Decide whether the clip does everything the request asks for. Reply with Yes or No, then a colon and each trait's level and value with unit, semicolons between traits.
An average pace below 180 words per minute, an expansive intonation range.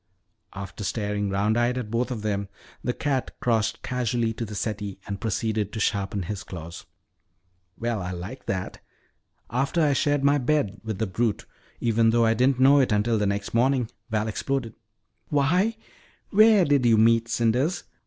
No: average, 170 wpm; average, 3.9 semitones